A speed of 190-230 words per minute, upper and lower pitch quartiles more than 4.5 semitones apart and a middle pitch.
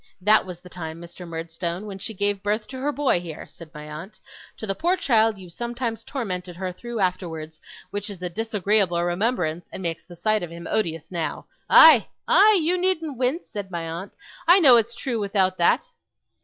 No: average, 195 wpm; average, 5.1 semitones; high, 195 Hz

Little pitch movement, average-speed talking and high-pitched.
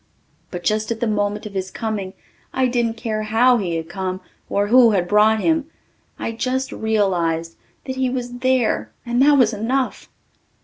No: average, 3.8 semitones; average, 175 wpm; high, 220 Hz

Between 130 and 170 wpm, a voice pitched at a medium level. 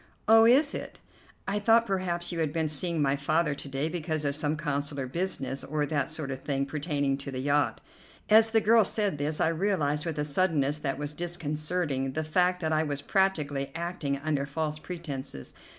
No: average, 195 wpm; medium, 155 Hz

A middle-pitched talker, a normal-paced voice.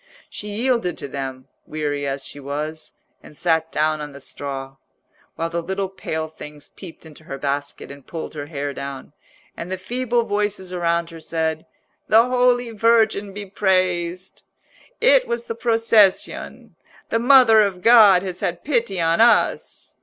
Yes: medium, 180 Hz; average, 160 wpm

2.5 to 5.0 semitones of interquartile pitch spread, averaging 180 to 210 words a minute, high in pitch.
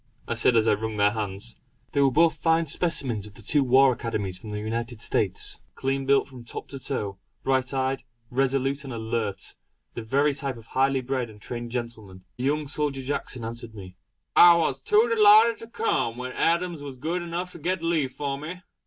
No: average, 4.6 semitones; average, 200 wpm; low, 135 Hz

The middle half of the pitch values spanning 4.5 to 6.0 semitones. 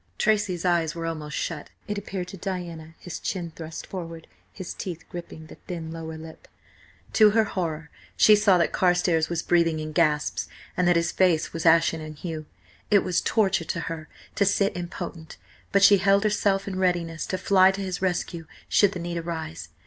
No: average, 2.7 semitones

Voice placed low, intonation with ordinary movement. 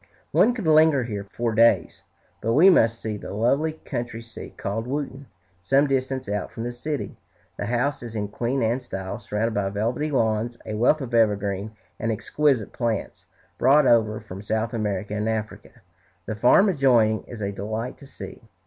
Yes: low, 115 Hz; average, 3.8 semitones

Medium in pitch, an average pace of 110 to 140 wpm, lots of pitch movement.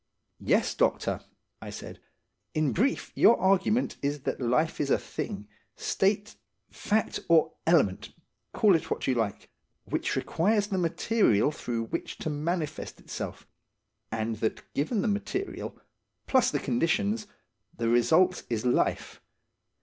Yes: medium, 160 Hz; slow, 135 wpm; wide, 8.4 semitones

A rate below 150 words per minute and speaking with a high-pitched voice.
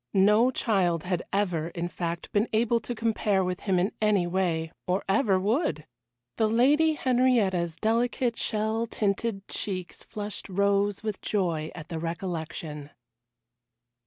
Yes: slow, 135 wpm; high, 200 Hz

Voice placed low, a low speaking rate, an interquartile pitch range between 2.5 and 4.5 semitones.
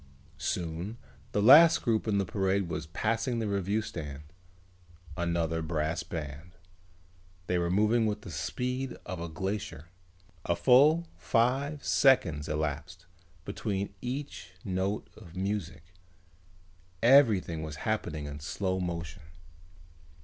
No: very low, 95 Hz; slow, 120 wpm; average, 5.1 semitones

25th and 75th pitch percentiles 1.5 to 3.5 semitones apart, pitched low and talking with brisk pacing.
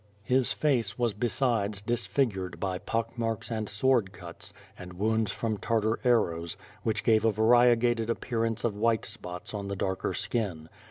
No: average, 2.8 semitones; low, 110 Hz; average, 155 wpm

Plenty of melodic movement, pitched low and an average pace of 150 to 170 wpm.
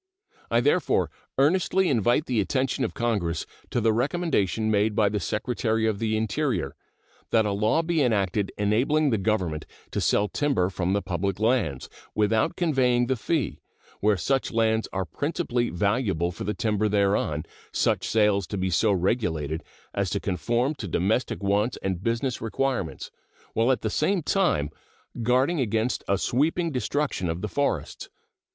No: average, 4.7 semitones; low, 110 Hz; average, 160 wpm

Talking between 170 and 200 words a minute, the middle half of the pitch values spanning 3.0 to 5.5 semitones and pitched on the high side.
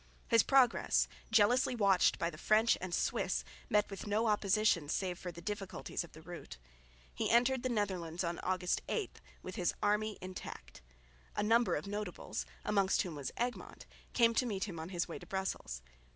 Yes: average, 180 wpm; average, 3.8 semitones; high, 200 Hz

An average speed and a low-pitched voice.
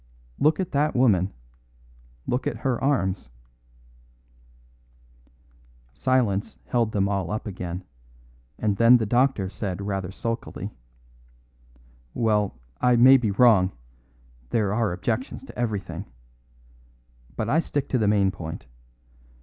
No: slow, 115 wpm; low, 105 Hz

